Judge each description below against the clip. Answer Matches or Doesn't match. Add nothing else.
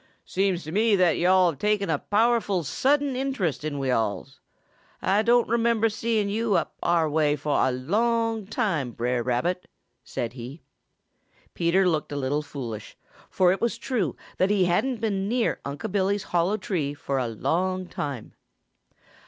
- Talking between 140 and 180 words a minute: Matches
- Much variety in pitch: Matches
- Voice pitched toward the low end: Doesn't match